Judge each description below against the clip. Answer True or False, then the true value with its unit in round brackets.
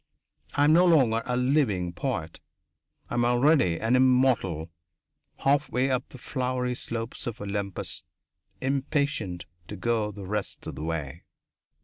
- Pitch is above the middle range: False (120 Hz)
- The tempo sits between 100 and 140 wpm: True (135 wpm)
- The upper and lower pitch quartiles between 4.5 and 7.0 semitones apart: True (5.0 semitones)